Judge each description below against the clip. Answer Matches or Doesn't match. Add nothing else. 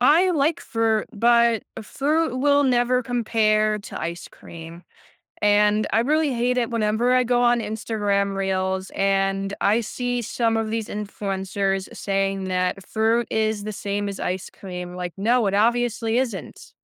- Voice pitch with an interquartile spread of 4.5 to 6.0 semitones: Doesn't match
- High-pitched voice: Matches